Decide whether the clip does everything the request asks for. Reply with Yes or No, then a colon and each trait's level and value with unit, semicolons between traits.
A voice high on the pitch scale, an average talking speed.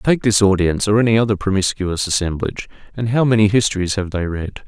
No: low, 100 Hz; average, 190 wpm